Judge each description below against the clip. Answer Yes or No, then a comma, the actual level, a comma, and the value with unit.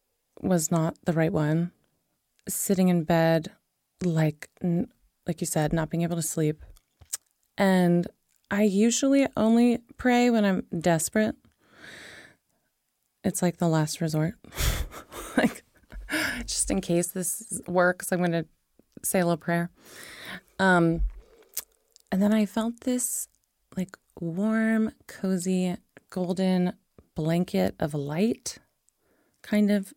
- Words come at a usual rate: No, slow, 115 wpm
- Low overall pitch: No, medium, 185 Hz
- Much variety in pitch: No, average, 4.0 semitones